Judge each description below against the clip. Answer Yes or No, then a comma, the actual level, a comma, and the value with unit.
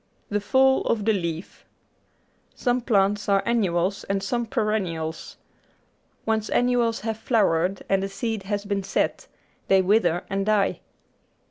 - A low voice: No, high, 205 Hz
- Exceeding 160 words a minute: No, slow, 135 wpm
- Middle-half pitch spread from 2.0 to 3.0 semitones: Yes, narrow, 2.6 semitones